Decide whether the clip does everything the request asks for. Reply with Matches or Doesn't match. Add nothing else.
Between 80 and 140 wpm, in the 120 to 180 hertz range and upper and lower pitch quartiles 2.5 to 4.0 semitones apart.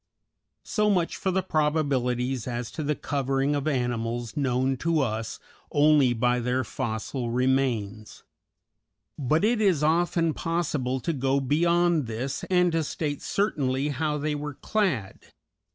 Doesn't match